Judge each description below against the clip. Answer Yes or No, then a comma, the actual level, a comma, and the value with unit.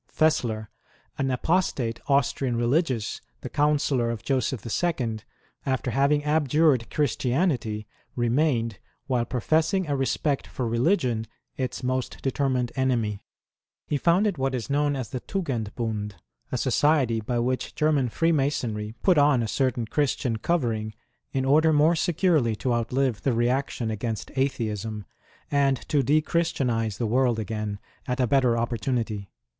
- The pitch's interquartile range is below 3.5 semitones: No, average, 4.1 semitones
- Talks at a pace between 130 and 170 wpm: Yes, slow, 135 wpm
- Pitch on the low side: Yes, low, 130 Hz